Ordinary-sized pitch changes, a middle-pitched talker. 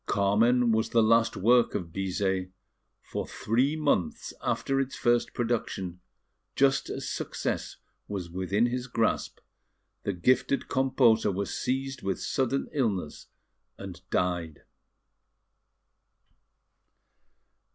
No: average, 5.0 semitones; low, 115 Hz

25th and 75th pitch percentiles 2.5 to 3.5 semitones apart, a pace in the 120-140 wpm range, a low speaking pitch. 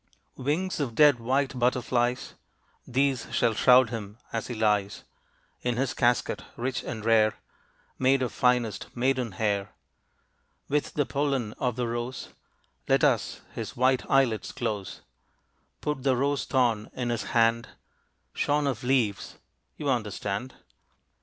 Yes: average, 2.8 semitones; slow, 135 wpm; low, 125 Hz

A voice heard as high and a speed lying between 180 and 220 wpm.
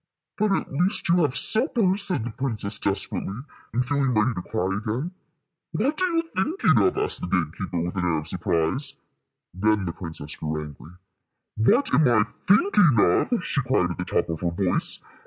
No: low, 110 Hz; average, 190 wpm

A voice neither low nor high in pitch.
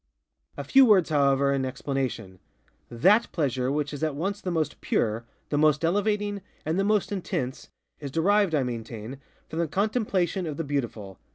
Yes: medium, 150 Hz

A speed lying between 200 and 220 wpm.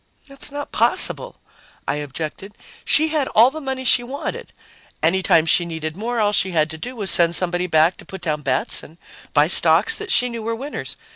Yes: fast, 205 wpm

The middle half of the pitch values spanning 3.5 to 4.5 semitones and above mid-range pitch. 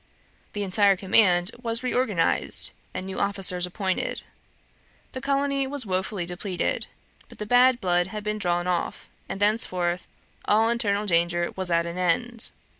Yes: average, 4.2 semitones; high, 195 Hz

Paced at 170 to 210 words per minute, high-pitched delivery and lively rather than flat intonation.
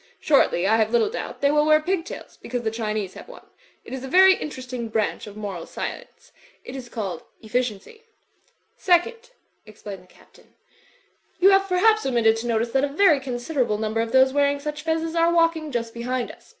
Yes: average, 200 wpm; very high, 260 Hz; wide, 6.4 semitones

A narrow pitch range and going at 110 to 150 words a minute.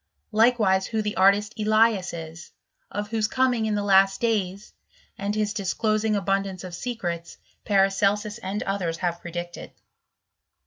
Yes: narrow, 2.3 semitones; slow, 135 wpm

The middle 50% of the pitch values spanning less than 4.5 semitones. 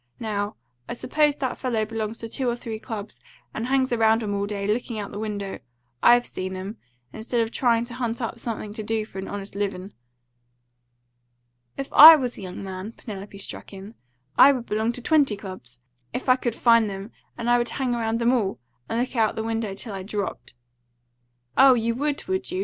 Yes: average, 3.1 semitones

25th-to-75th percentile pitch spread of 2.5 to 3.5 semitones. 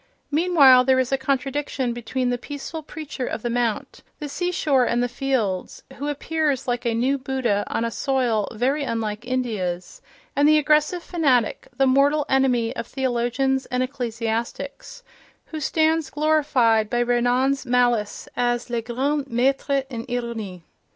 Yes: average, 3.0 semitones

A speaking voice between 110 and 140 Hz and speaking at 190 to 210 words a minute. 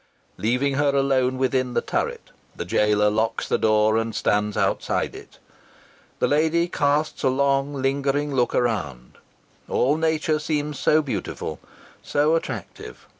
No: low, 135 Hz; slow, 135 wpm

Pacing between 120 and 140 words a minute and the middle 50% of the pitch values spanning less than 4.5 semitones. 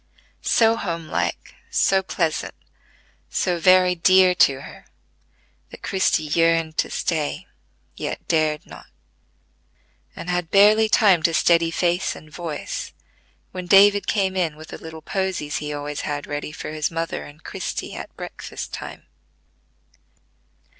Yes: slow, 135 wpm; average, 3.3 semitones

